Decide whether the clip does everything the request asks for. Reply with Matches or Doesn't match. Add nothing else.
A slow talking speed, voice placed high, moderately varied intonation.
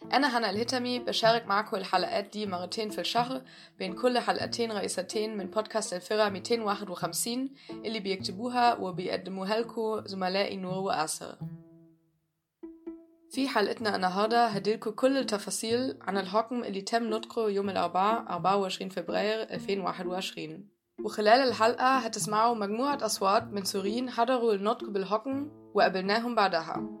Matches